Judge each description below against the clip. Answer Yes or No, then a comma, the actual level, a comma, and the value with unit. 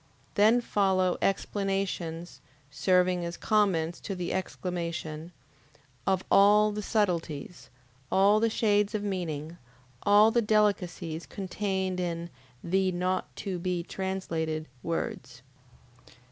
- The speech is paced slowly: Yes, slow, 105 wpm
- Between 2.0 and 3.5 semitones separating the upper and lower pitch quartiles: Yes, average, 3.0 semitones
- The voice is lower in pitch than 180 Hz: No, medium, 185 Hz